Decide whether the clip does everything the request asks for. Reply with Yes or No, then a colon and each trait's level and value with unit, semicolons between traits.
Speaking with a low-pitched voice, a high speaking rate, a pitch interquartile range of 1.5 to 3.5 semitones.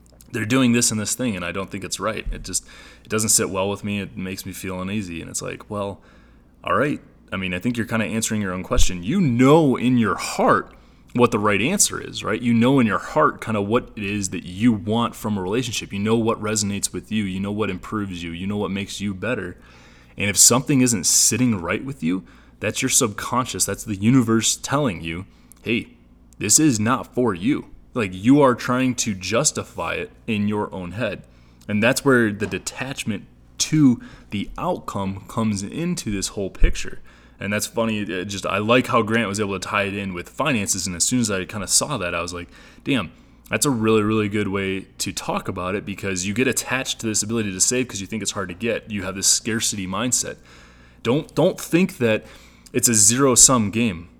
No: low, 105 Hz; fast, 225 wpm; average, 4.0 semitones